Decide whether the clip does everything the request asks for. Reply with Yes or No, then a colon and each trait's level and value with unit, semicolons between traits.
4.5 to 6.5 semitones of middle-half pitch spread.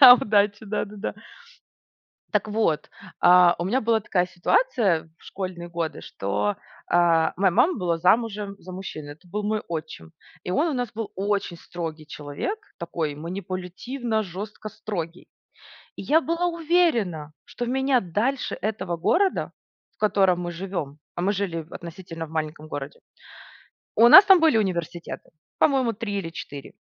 Yes: average, 4.9 semitones